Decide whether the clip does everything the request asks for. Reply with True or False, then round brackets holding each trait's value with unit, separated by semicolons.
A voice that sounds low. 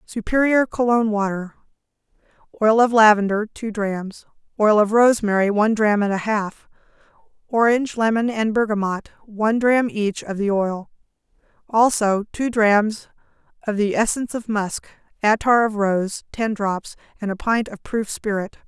False (215 Hz)